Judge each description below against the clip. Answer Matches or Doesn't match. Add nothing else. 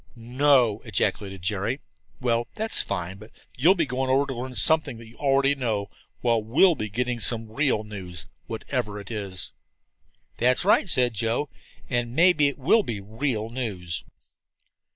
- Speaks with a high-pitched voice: Doesn't match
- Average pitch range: Matches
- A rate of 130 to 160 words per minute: Matches